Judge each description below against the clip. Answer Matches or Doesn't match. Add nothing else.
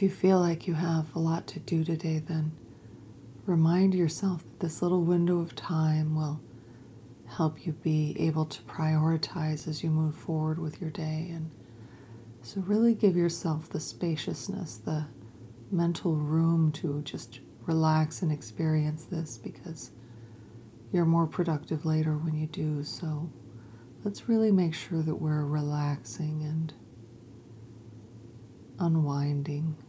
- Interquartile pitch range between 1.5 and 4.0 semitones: Doesn't match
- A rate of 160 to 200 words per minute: Doesn't match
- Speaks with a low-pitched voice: Doesn't match